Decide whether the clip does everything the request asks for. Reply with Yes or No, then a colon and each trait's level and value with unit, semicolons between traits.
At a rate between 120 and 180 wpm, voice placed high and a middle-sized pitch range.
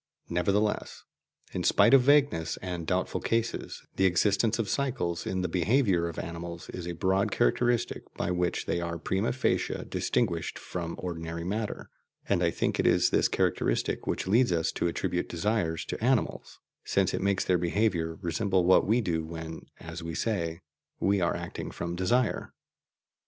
No: average, 165 wpm; very low, 90 Hz; average, 4.2 semitones